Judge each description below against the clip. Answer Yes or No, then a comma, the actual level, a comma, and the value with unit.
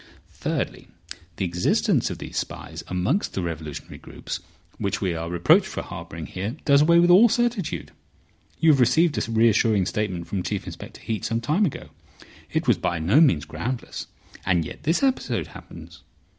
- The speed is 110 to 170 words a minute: Yes, average, 165 wpm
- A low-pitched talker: Yes, low, 110 Hz